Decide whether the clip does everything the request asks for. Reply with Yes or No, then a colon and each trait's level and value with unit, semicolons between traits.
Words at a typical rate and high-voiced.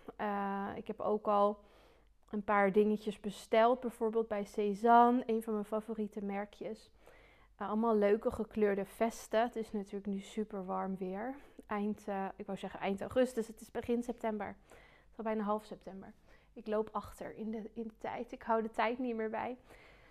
Yes: average, 180 wpm; high, 215 Hz